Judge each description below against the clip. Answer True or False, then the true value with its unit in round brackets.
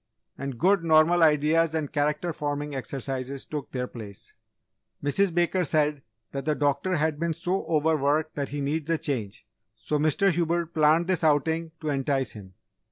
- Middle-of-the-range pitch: True (150 Hz)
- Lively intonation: False (2.8 semitones)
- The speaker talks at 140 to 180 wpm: True (165 wpm)